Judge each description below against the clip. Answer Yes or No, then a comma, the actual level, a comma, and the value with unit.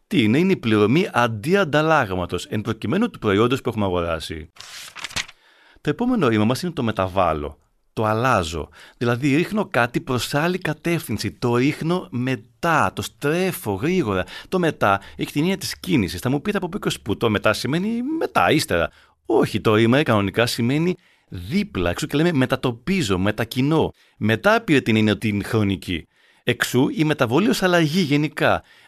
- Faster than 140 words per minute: Yes, average, 155 wpm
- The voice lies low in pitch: Yes, low, 130 Hz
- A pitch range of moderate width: No, wide, 7.3 semitones